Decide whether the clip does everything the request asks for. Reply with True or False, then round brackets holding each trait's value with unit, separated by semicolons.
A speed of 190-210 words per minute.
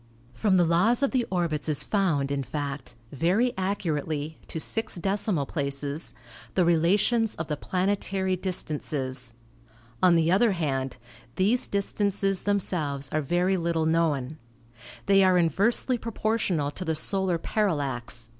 False (135 wpm)